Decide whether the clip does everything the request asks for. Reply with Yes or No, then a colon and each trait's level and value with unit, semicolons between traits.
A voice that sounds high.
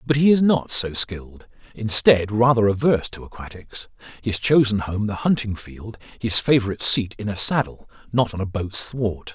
No: low, 110 Hz